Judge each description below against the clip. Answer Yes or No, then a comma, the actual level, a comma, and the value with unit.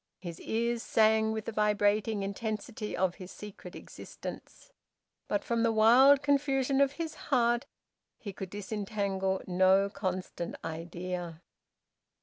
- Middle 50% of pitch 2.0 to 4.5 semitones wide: Yes, average, 3.7 semitones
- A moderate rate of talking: No, slow, 125 wpm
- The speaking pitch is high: Yes, high, 210 Hz